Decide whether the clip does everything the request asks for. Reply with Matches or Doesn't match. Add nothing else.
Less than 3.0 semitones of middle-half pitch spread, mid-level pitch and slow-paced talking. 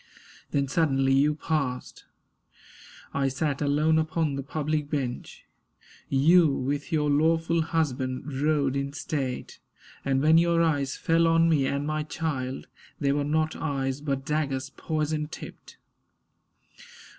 Matches